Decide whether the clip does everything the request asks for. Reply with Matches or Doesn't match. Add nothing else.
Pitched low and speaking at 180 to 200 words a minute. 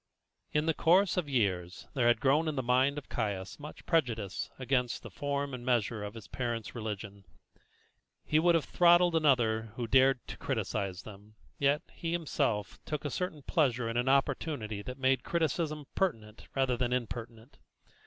Doesn't match